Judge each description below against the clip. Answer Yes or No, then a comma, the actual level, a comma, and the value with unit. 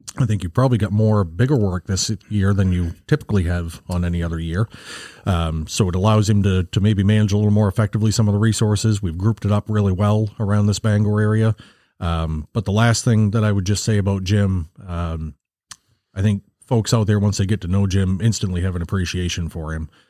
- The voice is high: No, low, 105 Hz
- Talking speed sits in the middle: No, fast, 225 wpm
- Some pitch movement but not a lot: Yes, average, 3.0 semitones